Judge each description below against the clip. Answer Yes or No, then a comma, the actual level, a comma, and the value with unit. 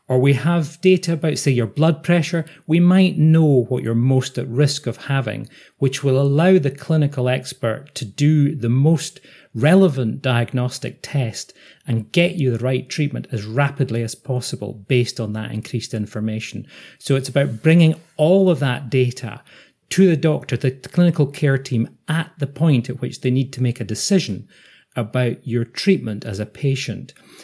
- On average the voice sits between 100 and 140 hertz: Yes, low, 135 Hz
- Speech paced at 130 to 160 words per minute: No, average, 175 wpm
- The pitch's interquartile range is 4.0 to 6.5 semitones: Yes, average, 4.5 semitones